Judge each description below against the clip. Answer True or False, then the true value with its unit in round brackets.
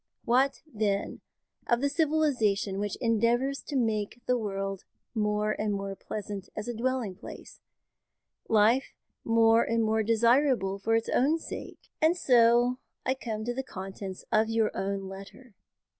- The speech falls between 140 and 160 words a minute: True (145 wpm)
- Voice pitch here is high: True (225 Hz)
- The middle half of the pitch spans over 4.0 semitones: False (3.4 semitones)